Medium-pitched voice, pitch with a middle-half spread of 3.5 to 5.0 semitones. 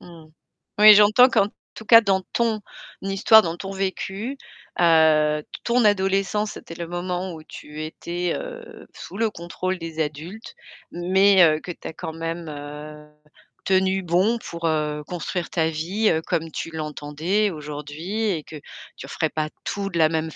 Yes: medium, 175 Hz; average, 3.9 semitones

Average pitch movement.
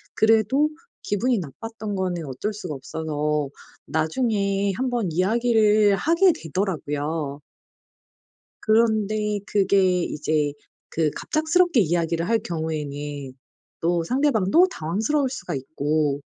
No: wide, 6.2 semitones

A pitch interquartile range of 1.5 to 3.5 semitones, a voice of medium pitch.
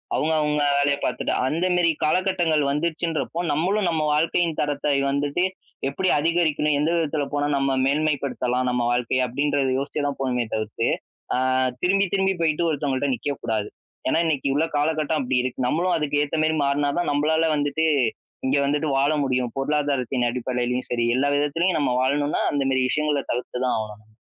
Yes: average, 3.2 semitones; medium, 145 Hz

